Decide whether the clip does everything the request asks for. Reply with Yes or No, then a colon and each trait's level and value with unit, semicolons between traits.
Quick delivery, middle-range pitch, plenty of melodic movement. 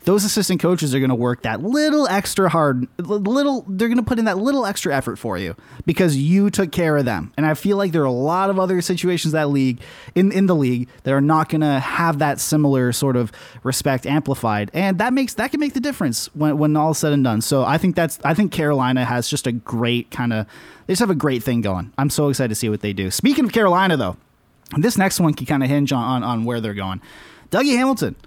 Yes: fast, 250 wpm; medium, 150 Hz; wide, 7.3 semitones